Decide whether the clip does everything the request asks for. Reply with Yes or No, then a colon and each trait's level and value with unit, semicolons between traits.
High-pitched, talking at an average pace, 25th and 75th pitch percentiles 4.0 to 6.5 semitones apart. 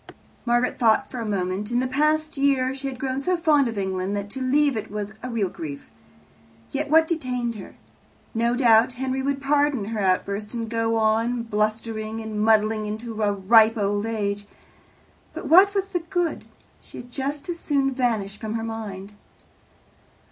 Yes: high, 230 Hz; average, 175 wpm; average, 4.3 semitones